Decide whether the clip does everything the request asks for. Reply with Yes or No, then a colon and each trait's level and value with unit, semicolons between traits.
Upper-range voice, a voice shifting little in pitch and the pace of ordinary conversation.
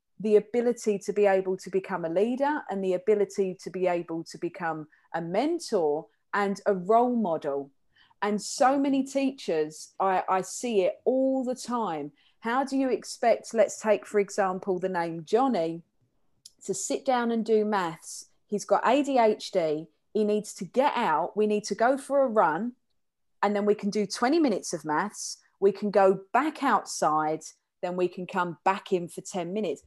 No: high, 200 Hz; average, 4.1 semitones; average, 180 wpm